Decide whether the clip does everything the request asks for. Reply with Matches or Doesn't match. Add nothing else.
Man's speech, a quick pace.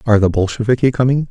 Doesn't match